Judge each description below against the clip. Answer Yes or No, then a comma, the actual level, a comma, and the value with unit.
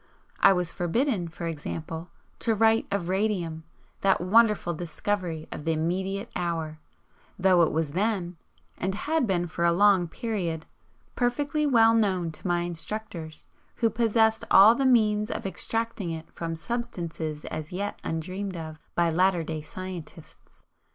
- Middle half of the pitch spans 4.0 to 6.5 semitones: Yes, average, 4.6 semitones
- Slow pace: No, average, 145 wpm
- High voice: No, medium, 180 Hz